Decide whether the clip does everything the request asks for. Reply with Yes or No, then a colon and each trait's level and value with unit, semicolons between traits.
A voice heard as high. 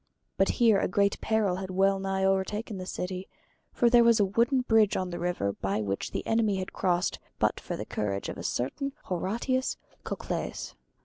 Yes: high, 195 Hz